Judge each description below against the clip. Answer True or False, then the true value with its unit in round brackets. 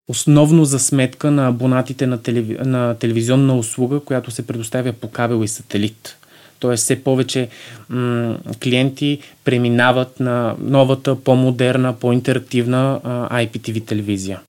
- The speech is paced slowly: True (110 wpm)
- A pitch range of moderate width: False (1.8 semitones)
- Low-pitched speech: True (125 Hz)